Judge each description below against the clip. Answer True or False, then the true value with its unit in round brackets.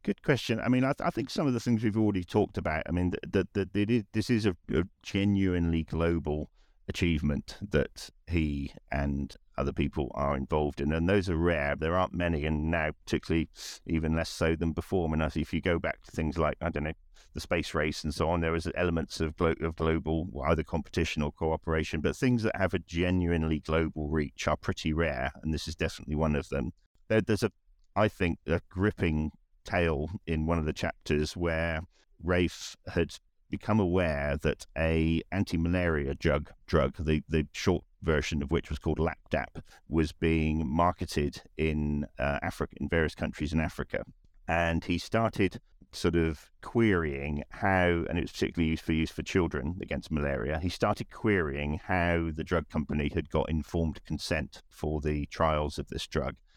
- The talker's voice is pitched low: True (80 Hz)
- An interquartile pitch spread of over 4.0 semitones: False (2.8 semitones)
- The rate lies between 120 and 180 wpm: False (190 wpm)